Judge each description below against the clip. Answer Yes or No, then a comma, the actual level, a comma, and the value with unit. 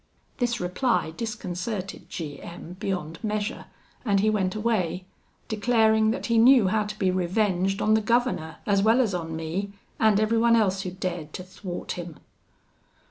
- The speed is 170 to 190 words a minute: No, average, 160 wpm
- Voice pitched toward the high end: Yes, high, 200 Hz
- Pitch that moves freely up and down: No, average, 3.4 semitones